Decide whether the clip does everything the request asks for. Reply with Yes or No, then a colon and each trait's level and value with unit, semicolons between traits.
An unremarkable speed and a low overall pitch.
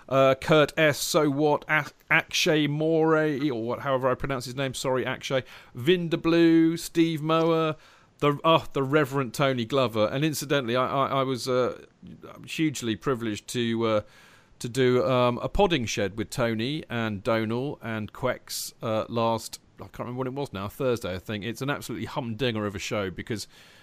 Yes: average, 175 wpm; low, 130 Hz